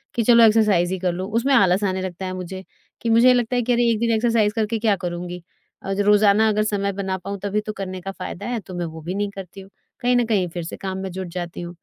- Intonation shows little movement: No, average, 3.2 semitones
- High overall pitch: Yes, high, 200 Hz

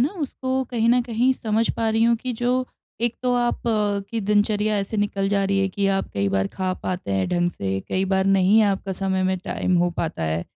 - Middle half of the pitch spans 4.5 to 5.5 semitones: No, average, 3.8 semitones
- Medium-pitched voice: No, high, 200 Hz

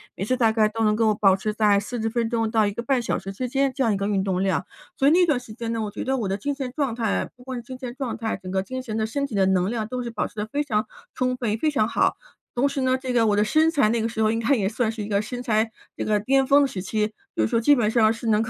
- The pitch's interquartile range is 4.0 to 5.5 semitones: No, average, 3.3 semitones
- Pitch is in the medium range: No, high, 225 Hz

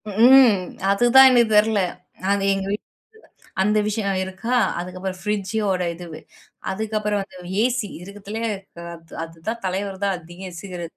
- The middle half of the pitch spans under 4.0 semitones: Yes, average, 2.9 semitones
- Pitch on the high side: Yes, high, 200 Hz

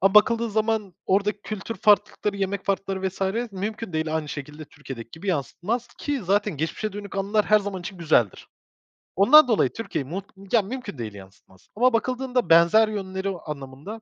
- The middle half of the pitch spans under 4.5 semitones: No, average, 5.0 semitones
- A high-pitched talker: Yes, high, 195 Hz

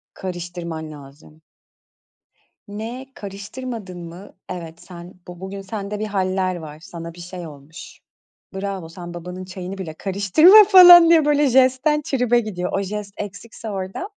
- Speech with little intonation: No, average, 4.3 semitones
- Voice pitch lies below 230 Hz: Yes, high, 190 Hz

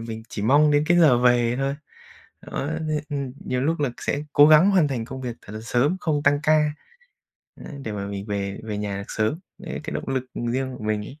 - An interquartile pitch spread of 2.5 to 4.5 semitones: No, average, 5.1 semitones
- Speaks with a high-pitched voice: No, low, 130 Hz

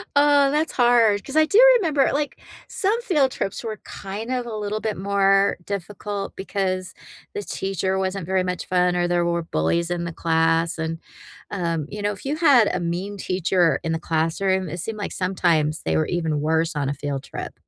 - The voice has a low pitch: No, high, 190 Hz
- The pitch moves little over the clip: No, average, 4.3 semitones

